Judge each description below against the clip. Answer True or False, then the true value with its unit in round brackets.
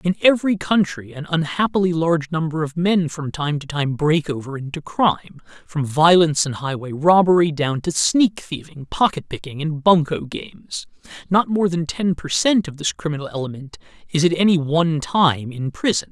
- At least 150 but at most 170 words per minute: False (180 wpm)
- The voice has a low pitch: False (160 Hz)